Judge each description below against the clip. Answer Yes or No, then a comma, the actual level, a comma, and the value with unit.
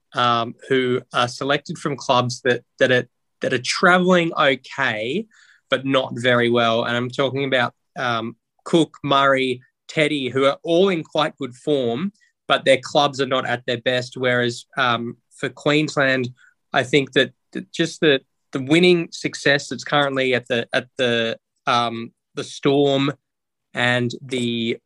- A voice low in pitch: Yes, low, 130 Hz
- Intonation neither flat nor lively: Yes, average, 3.1 semitones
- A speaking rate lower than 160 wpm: Yes, average, 150 wpm